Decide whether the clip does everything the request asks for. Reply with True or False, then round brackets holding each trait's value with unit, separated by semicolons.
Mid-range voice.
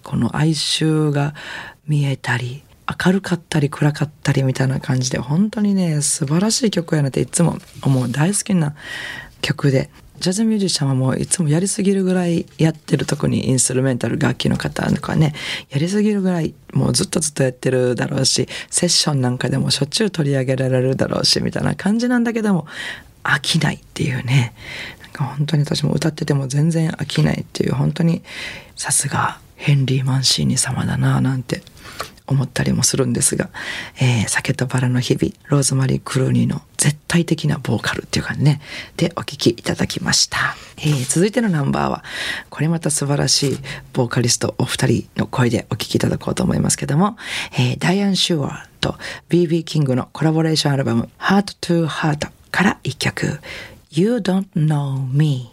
True (150 Hz)